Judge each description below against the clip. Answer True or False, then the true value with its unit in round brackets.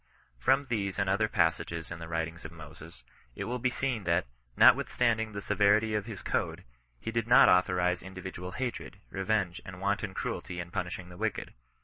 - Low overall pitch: True (95 Hz)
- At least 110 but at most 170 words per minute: False (185 wpm)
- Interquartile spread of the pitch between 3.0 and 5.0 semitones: True (3.9 semitones)